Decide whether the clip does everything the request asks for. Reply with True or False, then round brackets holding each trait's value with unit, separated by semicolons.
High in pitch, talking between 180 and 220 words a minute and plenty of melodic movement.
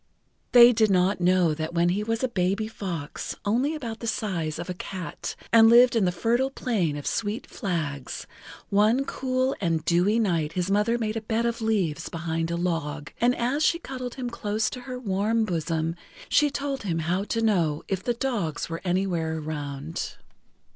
True (200 Hz; 185 wpm; 5.8 semitones)